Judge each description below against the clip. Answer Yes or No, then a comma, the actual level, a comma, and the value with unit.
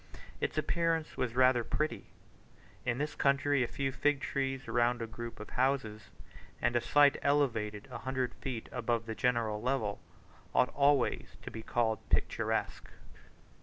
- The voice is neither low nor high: No, low, 125 Hz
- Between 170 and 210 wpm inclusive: No, average, 150 wpm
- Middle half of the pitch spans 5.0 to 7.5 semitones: No, average, 3.2 semitones